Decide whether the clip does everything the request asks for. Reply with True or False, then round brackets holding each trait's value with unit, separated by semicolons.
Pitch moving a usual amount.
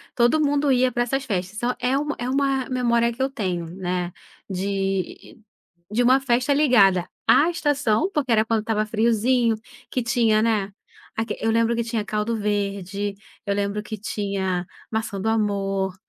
True (3.9 semitones)